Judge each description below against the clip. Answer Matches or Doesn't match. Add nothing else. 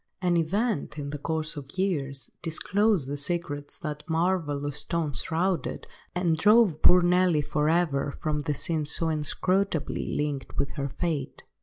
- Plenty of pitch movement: Doesn't match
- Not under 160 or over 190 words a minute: Doesn't match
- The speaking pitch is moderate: Matches